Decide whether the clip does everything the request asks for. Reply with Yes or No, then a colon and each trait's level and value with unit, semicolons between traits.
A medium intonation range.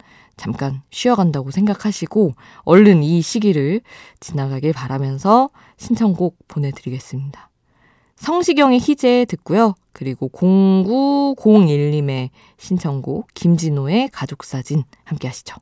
No: wide, 7.5 semitones